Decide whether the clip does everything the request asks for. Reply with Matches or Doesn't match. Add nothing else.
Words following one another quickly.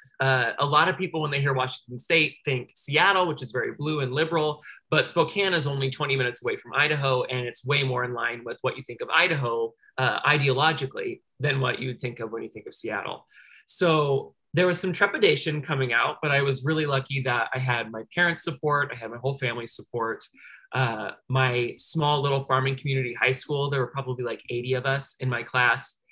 Matches